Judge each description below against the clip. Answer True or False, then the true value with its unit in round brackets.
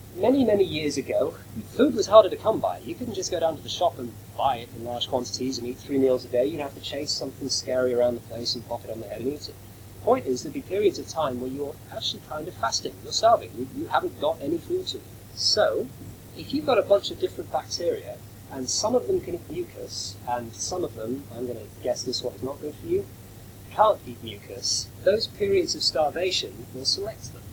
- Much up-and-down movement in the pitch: True (7.6 semitones)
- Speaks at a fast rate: True (240 wpm)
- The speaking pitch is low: True (130 Hz)